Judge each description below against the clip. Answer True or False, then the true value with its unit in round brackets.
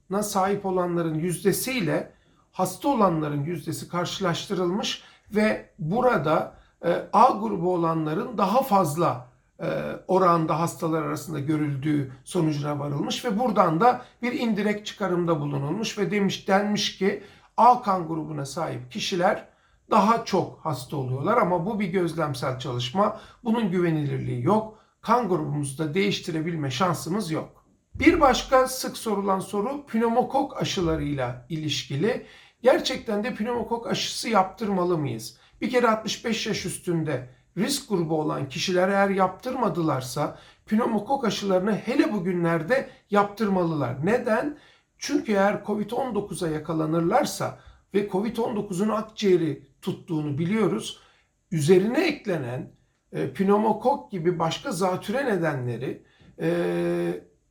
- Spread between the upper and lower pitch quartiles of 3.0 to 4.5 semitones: False (5.2 semitones)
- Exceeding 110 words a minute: False (105 wpm)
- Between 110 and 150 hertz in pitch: False (190 Hz)